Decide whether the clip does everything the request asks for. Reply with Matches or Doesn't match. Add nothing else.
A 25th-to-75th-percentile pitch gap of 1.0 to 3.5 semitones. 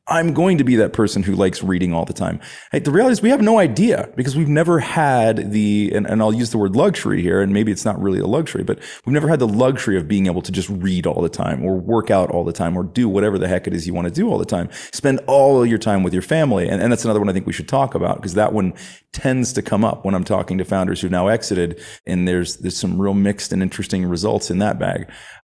Doesn't match